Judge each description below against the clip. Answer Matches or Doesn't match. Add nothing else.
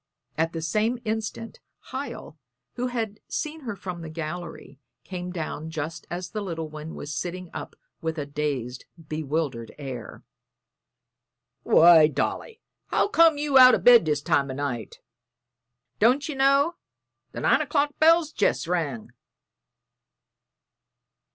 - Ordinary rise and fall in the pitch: Doesn't match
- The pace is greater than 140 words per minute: Doesn't match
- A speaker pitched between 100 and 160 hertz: Doesn't match